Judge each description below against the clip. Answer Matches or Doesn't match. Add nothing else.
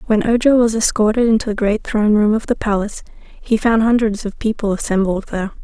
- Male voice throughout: Doesn't match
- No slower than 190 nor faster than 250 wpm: Matches